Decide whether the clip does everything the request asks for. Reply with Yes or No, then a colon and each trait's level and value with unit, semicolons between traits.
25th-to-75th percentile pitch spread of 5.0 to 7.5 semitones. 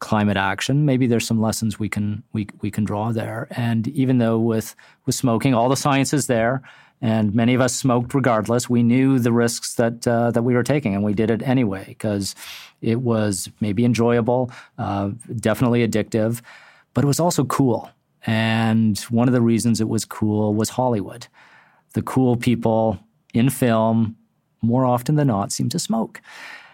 No: narrow, 2.4 semitones